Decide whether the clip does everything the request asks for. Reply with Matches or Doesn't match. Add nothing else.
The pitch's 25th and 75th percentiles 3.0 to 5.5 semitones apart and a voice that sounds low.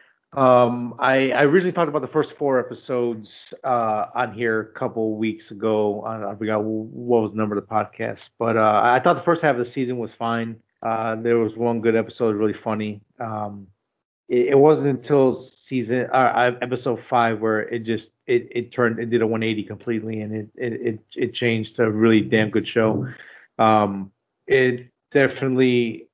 Doesn't match